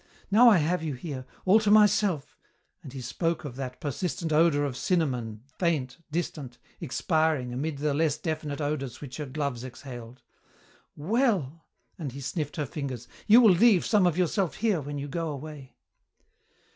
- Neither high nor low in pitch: Yes, medium, 150 Hz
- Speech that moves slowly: No, average, 165 wpm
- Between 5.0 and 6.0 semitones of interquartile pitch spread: No, average, 4.4 semitones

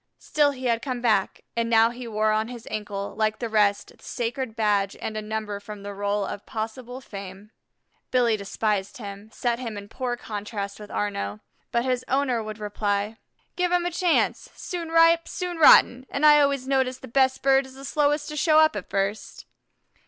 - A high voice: Yes, high, 230 Hz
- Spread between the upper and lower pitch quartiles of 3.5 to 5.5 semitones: Yes, average, 4.2 semitones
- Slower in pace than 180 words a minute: No, average, 190 wpm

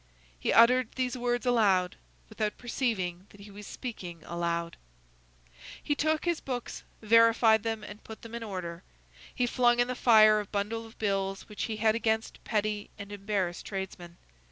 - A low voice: No, high, 215 Hz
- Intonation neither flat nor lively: Yes, average, 3.2 semitones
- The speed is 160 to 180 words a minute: Yes, average, 165 wpm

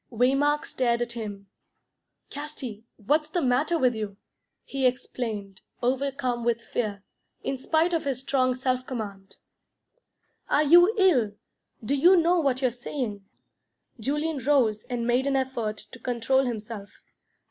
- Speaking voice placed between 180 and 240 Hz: No, very high, 255 Hz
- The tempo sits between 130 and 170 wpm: Yes, slow, 135 wpm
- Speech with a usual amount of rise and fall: Yes, average, 3.6 semitones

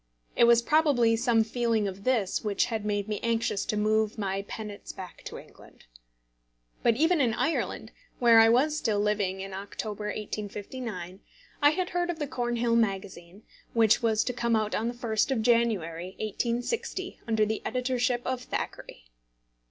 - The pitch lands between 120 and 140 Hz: No, high, 225 Hz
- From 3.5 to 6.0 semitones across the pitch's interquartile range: No, average, 2.7 semitones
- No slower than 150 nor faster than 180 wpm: Yes, average, 165 wpm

